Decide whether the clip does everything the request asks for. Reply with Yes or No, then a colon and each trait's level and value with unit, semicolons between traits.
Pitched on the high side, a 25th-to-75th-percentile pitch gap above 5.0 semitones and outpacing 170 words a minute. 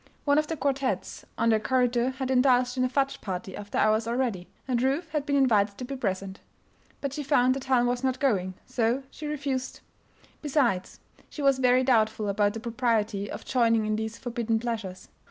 No: high, 245 Hz; average, 3.5 semitones; average, 190 wpm